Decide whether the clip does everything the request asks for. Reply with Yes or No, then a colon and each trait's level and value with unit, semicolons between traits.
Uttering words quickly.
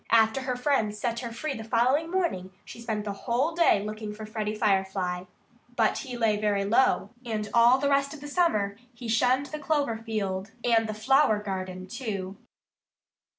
No: average, 180 wpm